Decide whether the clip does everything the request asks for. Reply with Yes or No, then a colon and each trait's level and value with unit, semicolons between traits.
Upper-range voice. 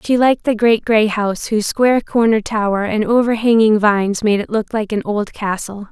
Yes: high, 215 Hz